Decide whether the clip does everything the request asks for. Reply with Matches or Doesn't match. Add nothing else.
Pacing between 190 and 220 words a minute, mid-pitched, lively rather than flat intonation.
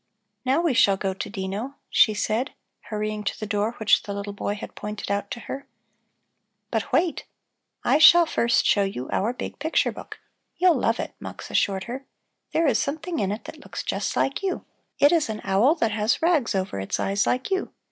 Doesn't match